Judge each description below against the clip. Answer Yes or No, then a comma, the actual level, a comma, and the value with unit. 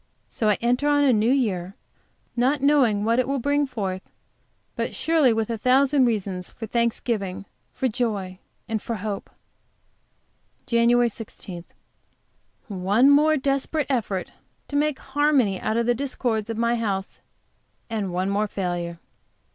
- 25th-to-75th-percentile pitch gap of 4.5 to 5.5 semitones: Yes, average, 4.8 semitones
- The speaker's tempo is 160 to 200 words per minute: No, average, 145 wpm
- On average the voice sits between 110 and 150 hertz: No, high, 230 Hz